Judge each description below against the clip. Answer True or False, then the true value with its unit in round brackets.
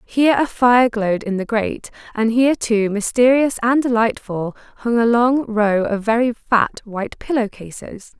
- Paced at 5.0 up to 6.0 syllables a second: False (4.7 syllables/s)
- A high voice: True (230 Hz)